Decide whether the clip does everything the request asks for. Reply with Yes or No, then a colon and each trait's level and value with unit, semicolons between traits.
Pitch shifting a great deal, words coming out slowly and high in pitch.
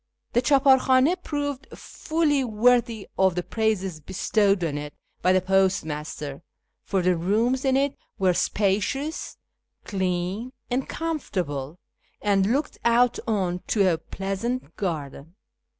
Yes: wide, 6.1 semitones; slow, 125 wpm; high, 200 Hz